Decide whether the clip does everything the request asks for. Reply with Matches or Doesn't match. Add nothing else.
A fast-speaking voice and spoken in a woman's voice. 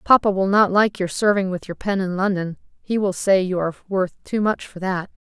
Matches